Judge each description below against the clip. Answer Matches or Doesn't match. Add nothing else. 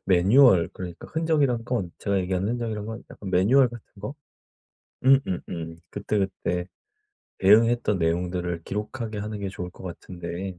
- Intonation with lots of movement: Doesn't match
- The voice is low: Matches